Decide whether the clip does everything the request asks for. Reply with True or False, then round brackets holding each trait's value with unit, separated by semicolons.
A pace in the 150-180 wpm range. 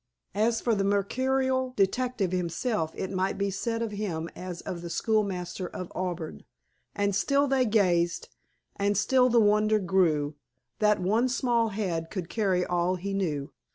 True (160 wpm)